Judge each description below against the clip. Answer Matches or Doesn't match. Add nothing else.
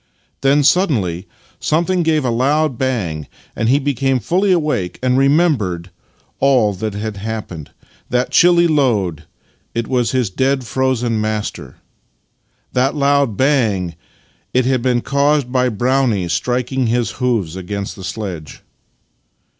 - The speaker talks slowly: Matches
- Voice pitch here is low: Matches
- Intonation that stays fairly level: Doesn't match